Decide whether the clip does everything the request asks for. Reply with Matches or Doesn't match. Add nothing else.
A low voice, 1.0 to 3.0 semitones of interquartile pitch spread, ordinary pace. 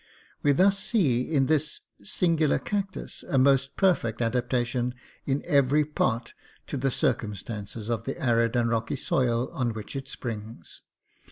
Doesn't match